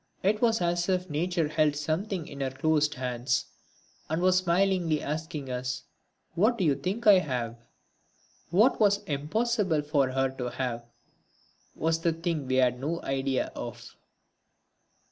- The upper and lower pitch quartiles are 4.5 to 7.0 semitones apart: Yes, wide, 5.4 semitones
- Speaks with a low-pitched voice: No, medium, 155 Hz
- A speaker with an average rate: Yes, average, 145 wpm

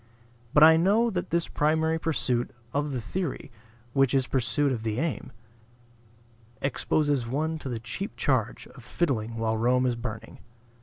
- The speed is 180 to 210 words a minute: No, average, 160 wpm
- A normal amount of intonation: Yes, average, 5.0 semitones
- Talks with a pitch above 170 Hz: No, low, 135 Hz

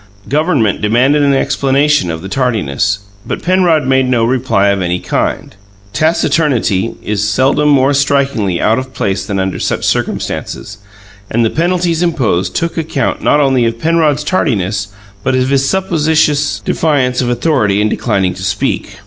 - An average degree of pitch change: No, wide, 6.1 semitones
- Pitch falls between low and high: No, low, 130 Hz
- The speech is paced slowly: No, average, 155 wpm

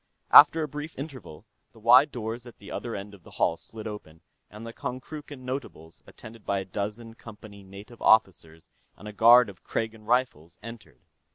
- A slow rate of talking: No, average, 180 wpm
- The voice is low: Yes, low, 110 Hz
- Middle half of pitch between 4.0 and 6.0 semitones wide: No, average, 3.6 semitones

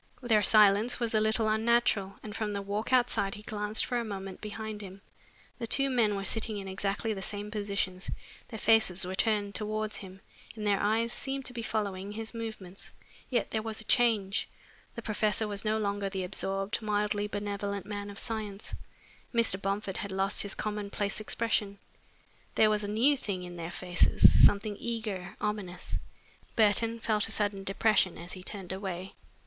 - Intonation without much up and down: Yes, narrow, 2.0 semitones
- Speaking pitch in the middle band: No, high, 210 Hz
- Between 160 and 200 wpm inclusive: Yes, average, 175 wpm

